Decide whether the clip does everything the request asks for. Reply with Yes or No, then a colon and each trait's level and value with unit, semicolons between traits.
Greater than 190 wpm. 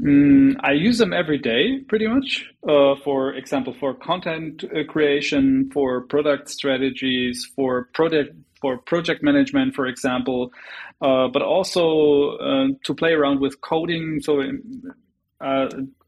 No: slow, 135 wpm